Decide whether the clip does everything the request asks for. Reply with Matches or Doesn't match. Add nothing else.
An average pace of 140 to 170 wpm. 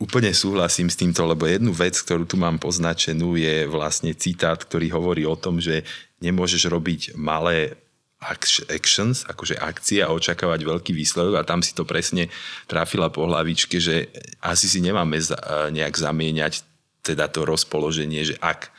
Matches